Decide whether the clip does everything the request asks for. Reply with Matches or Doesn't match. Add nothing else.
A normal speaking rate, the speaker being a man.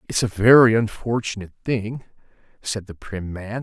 Matches